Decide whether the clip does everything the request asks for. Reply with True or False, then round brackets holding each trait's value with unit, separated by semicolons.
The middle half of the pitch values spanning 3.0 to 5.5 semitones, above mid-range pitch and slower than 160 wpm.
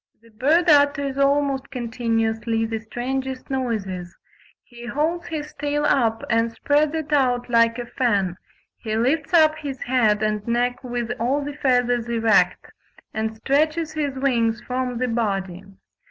True (3.9 semitones; 245 Hz; 145 wpm)